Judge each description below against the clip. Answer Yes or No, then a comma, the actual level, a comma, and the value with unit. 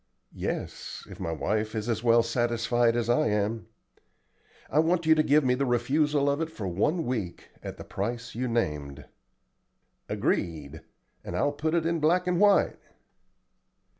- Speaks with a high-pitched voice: No, low, 120 Hz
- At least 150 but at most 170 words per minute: Yes, average, 165 wpm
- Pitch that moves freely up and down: Yes, wide, 5.9 semitones